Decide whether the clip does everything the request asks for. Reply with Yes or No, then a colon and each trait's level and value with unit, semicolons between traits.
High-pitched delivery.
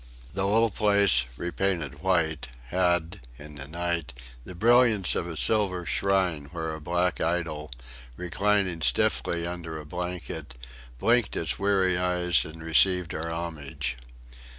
No: very low, 85 Hz